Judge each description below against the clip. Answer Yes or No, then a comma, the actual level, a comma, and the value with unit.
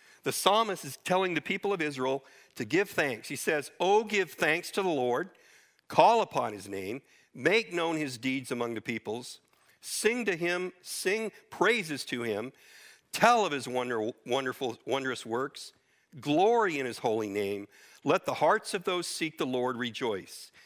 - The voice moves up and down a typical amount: No, wide, 7.7 semitones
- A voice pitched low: No, medium, 165 Hz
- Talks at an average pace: Yes, average, 170 wpm